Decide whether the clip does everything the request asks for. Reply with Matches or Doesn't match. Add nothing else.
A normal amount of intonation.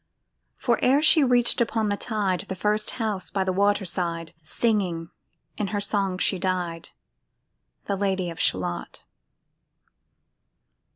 Matches